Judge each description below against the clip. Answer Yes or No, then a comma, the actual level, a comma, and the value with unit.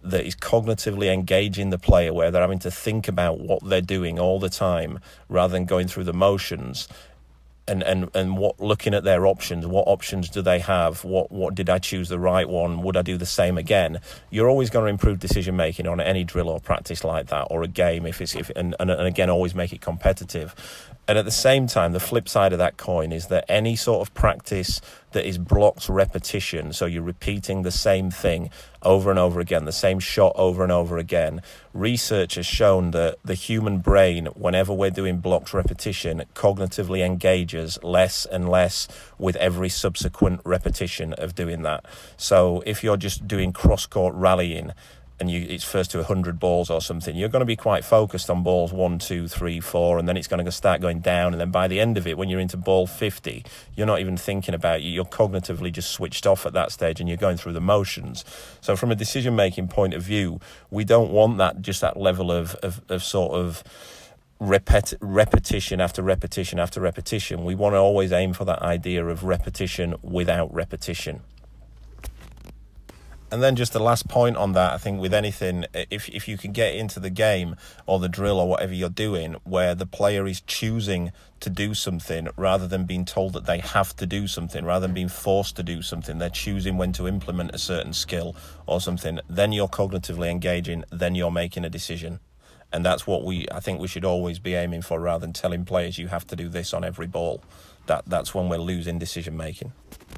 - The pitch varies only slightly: Yes, narrow, 2.1 semitones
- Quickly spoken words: Yes, fast, 210 wpm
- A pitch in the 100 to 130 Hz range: No, very low, 90 Hz